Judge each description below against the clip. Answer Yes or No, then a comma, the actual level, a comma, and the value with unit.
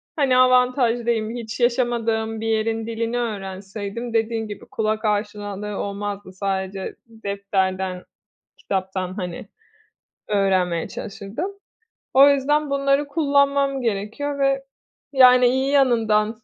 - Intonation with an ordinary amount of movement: Yes, average, 4.1 semitones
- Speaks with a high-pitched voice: Yes, high, 225 Hz